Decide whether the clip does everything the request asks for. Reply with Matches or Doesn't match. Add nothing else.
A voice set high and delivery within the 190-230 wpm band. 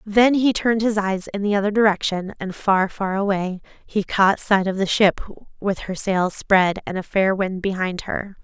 Matches